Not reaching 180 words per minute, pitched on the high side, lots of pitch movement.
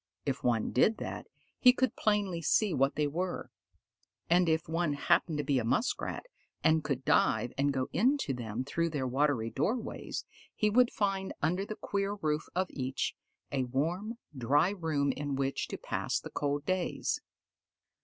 No: average, 165 wpm; medium, 155 Hz; wide, 5.9 semitones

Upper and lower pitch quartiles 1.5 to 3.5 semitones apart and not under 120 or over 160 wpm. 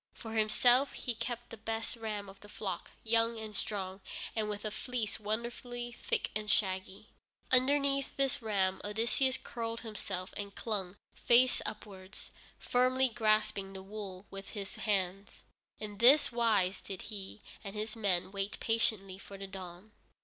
Yes: average, 3.0 semitones; average, 150 wpm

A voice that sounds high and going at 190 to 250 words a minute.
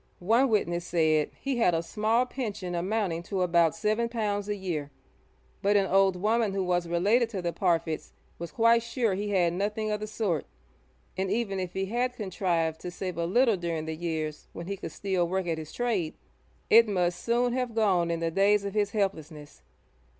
Yes: high, 195 Hz; average, 195 wpm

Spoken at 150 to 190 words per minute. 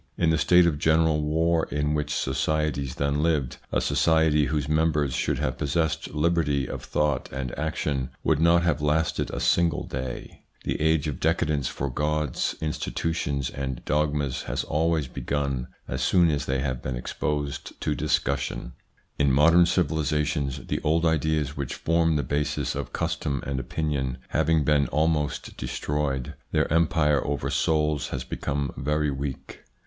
Yes: average, 155 wpm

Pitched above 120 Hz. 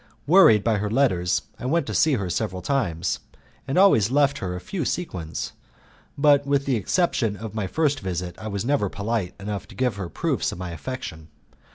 No: low, 110 Hz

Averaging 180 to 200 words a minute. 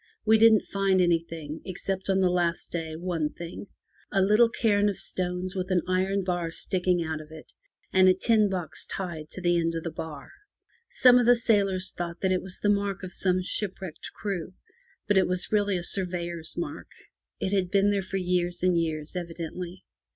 Yes: average, 195 wpm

